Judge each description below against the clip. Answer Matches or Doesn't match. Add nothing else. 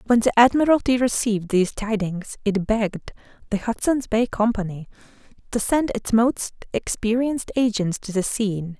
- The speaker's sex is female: Matches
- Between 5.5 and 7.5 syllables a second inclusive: Doesn't match